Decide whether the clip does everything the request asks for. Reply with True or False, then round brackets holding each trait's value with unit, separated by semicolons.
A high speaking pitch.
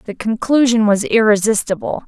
True (220 Hz)